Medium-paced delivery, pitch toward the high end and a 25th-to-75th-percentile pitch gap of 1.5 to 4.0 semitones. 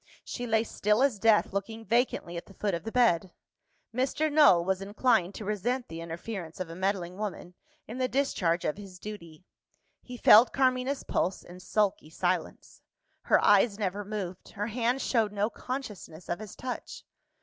No: average, 170 wpm; high, 210 Hz; average, 4.7 semitones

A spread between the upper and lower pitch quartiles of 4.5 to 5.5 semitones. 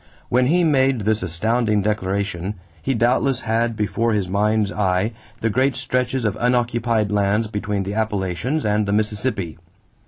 No: average, 3.2 semitones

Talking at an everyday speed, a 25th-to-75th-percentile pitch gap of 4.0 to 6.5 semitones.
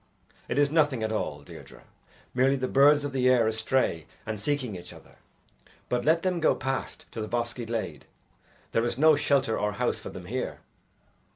Yes: average, 185 wpm; average, 4.4 semitones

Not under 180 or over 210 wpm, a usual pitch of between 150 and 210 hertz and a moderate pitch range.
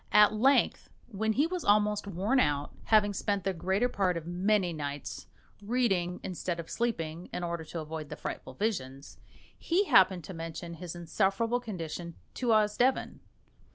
No: average, 155 wpm; high, 190 Hz; average, 4.3 semitones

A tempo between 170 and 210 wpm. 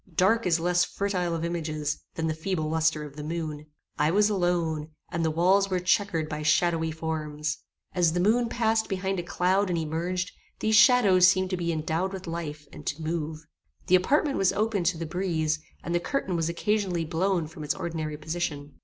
Yes: average, 195 wpm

